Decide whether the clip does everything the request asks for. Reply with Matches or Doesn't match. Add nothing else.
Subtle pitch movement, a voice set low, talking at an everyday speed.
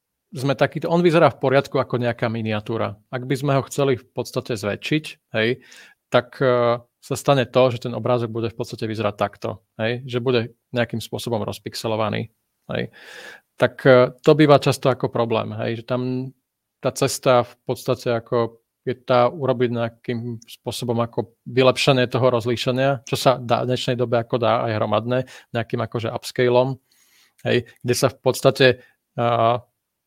Matches